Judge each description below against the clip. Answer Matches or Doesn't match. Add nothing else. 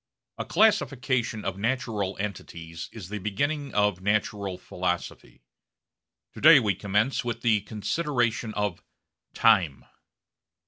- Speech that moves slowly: Matches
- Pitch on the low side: Matches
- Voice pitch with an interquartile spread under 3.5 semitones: Doesn't match